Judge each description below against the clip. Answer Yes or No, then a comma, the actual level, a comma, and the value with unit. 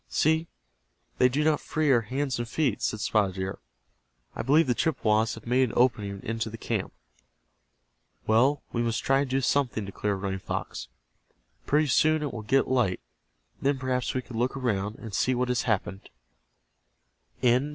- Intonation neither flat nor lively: Yes, average, 3.8 semitones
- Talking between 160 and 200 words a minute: Yes, average, 170 wpm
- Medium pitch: No, low, 125 Hz